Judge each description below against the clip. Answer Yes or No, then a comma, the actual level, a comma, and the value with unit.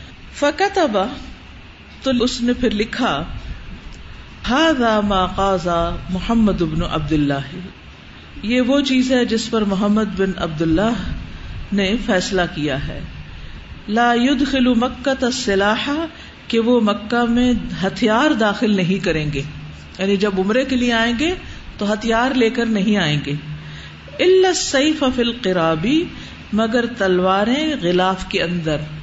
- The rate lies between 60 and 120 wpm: No, average, 130 wpm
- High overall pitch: Yes, high, 210 Hz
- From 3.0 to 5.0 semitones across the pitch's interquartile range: No, wide, 5.6 semitones